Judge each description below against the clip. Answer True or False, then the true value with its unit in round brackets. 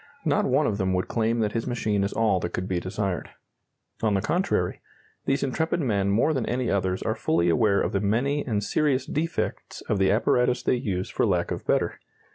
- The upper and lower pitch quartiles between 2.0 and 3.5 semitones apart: False (4.8 semitones)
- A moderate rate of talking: False (210 wpm)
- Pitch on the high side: False (110 Hz)